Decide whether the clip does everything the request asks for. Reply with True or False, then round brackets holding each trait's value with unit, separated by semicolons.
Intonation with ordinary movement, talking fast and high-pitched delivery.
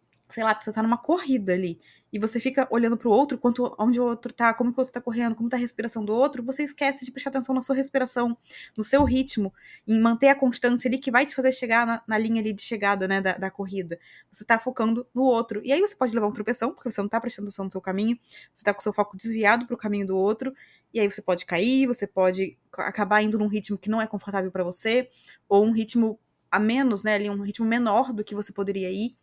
True (3.2 semitones; 260 wpm; 225 Hz)